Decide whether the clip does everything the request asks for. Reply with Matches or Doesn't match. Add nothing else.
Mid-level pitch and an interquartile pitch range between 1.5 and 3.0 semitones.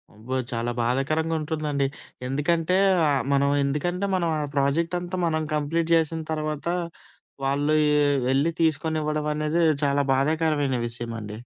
Matches